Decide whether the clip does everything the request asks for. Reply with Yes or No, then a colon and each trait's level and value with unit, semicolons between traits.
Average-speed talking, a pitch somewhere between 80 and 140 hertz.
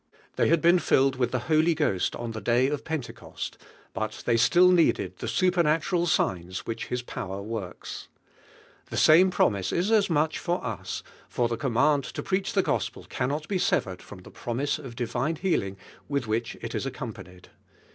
Yes: average, 180 wpm; low, 135 Hz